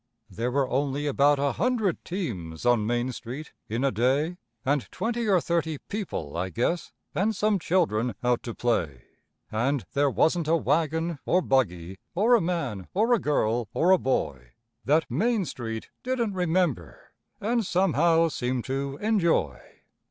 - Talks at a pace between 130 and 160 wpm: Yes, average, 155 wpm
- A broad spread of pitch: Yes, wide, 7.0 semitones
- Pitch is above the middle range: No, medium, 145 Hz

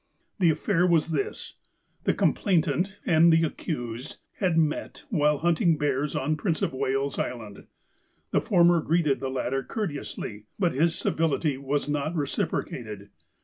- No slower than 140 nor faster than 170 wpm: Yes, average, 145 wpm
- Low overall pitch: No, medium, 150 Hz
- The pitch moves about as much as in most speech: Yes, average, 3.9 semitones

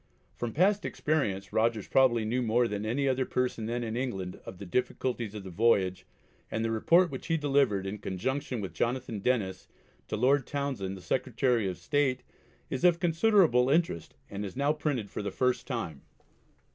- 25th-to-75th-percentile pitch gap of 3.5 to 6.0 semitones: Yes, average, 5.1 semitones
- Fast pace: No, average, 180 wpm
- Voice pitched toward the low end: Yes, low, 120 Hz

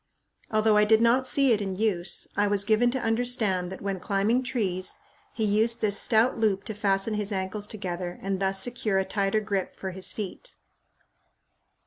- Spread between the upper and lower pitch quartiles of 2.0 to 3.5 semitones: Yes, narrow, 2.6 semitones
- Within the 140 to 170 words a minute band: No, average, 180 wpm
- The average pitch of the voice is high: Yes, high, 210 Hz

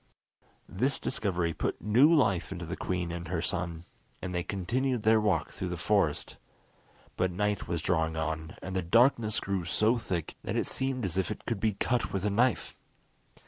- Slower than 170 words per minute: No, average, 185 wpm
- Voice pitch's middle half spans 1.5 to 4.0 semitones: No, average, 4.4 semitones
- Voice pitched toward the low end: Yes, very low, 95 Hz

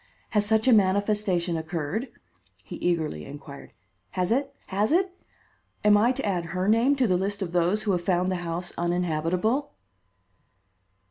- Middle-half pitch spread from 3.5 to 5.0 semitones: Yes, average, 4.0 semitones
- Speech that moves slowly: No, average, 155 wpm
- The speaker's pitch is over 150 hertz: Yes, high, 190 Hz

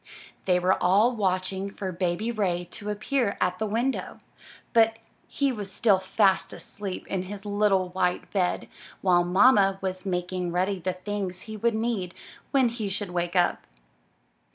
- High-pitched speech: Yes, high, 195 Hz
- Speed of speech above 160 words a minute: No, average, 155 wpm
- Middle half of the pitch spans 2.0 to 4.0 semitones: Yes, average, 2.8 semitones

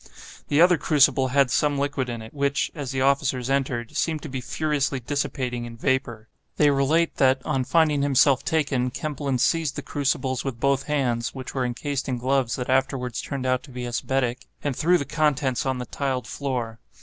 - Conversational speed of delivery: Yes, average, 190 wpm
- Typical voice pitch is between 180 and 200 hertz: No, low, 135 Hz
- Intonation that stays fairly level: Yes, narrow, 2.3 semitones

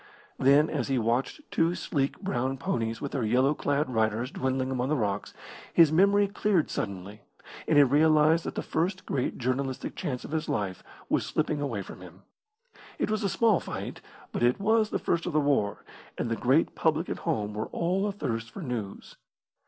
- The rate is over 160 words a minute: Yes, average, 190 wpm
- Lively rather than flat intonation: Yes, wide, 5.8 semitones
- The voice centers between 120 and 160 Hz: Yes, medium, 140 Hz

